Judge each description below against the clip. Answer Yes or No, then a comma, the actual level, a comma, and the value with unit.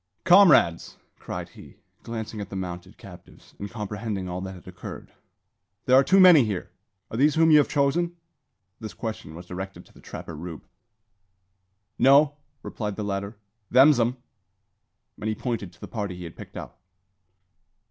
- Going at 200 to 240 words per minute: No, average, 165 wpm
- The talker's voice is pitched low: Yes, low, 110 Hz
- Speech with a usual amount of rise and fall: No, wide, 6.5 semitones